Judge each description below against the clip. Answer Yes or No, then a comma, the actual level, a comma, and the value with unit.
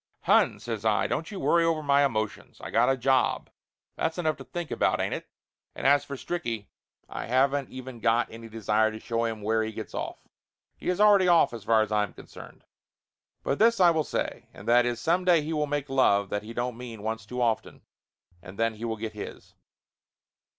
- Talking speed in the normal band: No, fast, 215 wpm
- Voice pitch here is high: No, low, 120 Hz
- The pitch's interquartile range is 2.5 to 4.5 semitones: No, average, 5.1 semitones